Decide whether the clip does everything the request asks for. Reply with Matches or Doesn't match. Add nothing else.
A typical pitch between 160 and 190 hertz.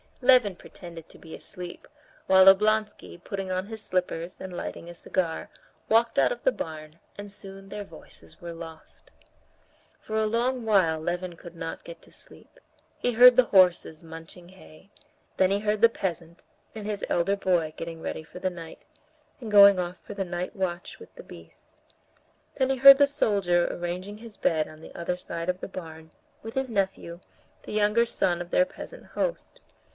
Matches